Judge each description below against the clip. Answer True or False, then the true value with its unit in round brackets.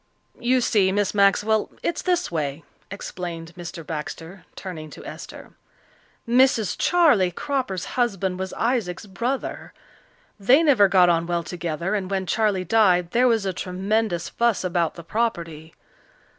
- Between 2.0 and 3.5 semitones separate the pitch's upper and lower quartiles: False (4.7 semitones)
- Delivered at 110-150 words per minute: True (140 wpm)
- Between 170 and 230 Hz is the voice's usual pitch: True (190 Hz)